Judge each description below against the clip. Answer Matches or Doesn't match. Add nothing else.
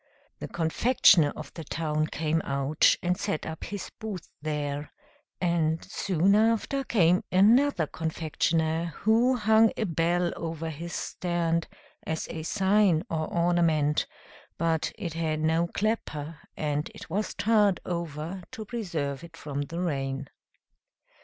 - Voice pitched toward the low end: Doesn't match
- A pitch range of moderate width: Matches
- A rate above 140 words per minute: Doesn't match